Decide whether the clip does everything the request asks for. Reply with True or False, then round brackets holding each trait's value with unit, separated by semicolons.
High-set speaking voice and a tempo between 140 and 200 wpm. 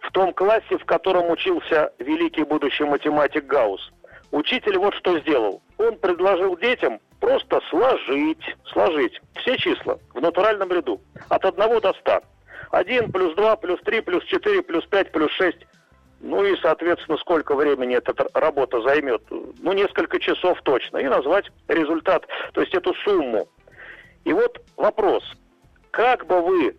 True (315 Hz; 145 wpm)